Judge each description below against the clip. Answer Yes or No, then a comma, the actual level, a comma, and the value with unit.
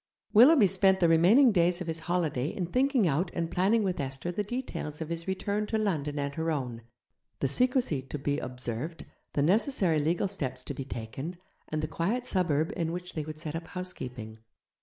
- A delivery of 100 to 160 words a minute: No, average, 195 wpm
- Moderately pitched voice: Yes, medium, 165 Hz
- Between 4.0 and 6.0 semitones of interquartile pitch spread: Yes, average, 4.9 semitones